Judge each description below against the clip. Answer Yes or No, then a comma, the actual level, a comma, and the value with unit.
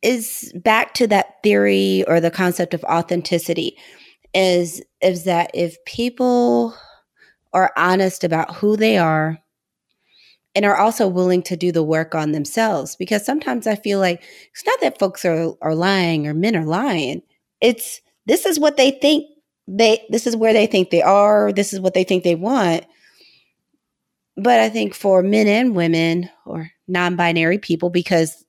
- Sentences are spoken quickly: No, average, 165 wpm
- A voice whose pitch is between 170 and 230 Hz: Yes, medium, 185 Hz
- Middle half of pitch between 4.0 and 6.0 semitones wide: Yes, average, 4.5 semitones